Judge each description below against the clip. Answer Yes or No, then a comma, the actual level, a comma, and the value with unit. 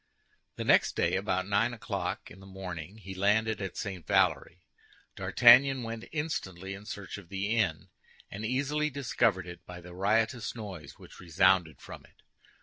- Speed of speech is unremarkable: Yes, average, 160 wpm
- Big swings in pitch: No, average, 3.7 semitones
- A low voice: Yes, low, 100 Hz